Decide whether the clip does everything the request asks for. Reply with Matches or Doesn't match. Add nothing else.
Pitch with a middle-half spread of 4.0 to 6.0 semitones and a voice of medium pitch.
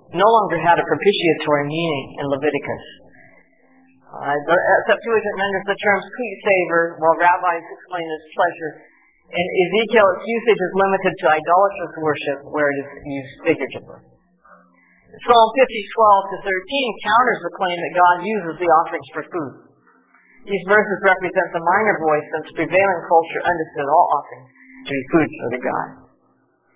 Matches